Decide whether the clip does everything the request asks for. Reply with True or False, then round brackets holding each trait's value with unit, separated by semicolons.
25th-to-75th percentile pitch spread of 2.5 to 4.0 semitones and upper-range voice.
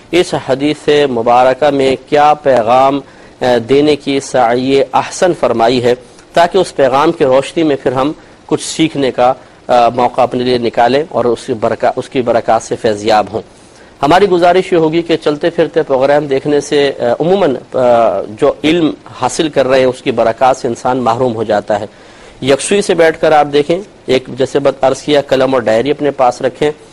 False (3.2 semitones; 135 Hz)